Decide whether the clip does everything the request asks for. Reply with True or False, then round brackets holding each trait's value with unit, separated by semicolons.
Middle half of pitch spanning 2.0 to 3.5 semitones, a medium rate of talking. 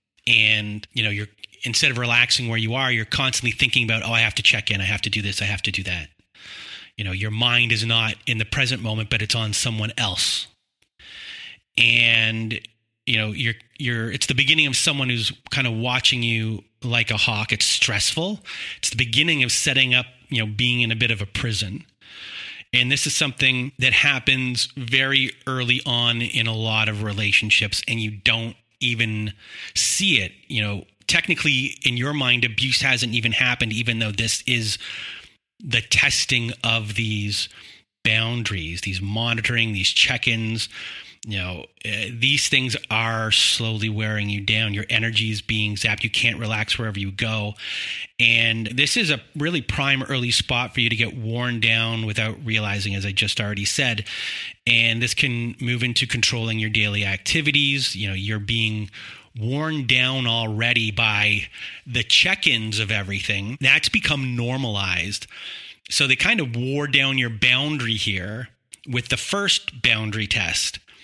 True (2.8 semitones; 170 wpm)